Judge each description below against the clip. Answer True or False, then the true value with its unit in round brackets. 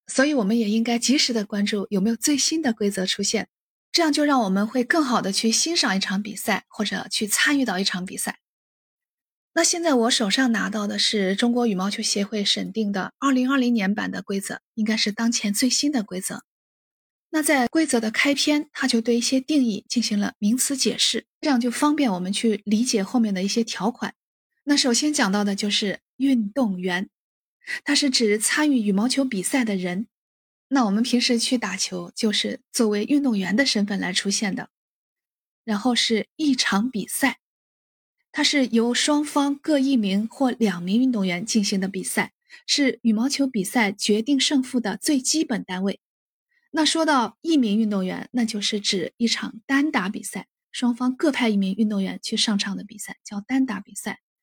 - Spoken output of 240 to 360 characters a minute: True (270 characters per minute)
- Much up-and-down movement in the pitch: False (4.7 semitones)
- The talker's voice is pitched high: True (230 Hz)